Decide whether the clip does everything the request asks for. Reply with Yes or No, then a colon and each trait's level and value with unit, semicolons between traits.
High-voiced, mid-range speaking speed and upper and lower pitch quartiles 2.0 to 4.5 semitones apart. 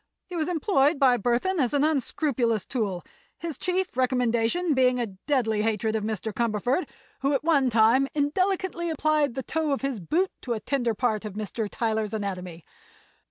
No: very high, 250 Hz; average, 170 wpm; wide, 5.6 semitones